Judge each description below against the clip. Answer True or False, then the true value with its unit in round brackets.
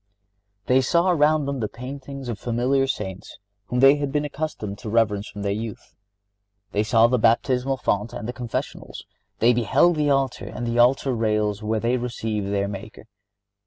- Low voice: True (120 Hz)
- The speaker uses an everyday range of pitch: True (4.1 semitones)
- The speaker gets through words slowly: False (180 wpm)